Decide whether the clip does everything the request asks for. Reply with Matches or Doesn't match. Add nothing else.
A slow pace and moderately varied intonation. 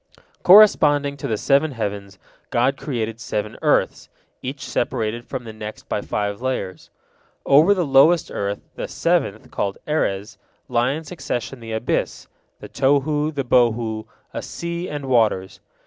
Doesn't match